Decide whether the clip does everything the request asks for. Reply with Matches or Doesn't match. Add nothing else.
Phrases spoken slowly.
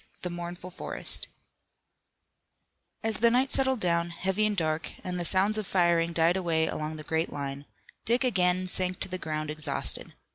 Doesn't match